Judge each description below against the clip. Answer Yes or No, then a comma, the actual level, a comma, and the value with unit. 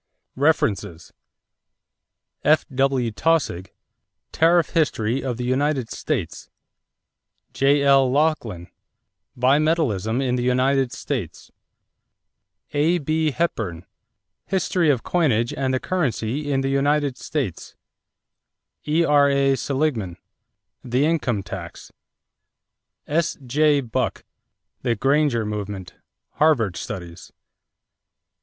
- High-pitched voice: No, low, 135 Hz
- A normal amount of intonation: Yes, average, 4.7 semitones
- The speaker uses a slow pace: Yes, slow, 80 wpm